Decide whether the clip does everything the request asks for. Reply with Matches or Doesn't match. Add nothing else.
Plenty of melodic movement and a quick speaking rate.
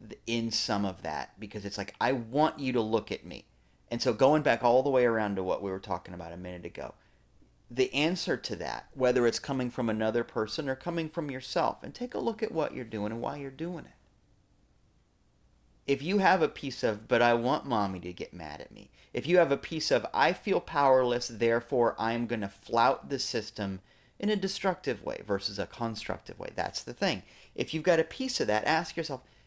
Matches